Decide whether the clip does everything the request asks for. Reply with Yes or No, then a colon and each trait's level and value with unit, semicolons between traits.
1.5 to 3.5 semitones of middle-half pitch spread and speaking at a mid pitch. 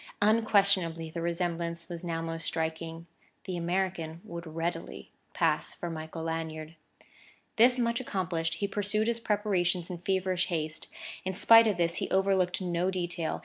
Yes: average, 2.7 semitones; medium, 175 Hz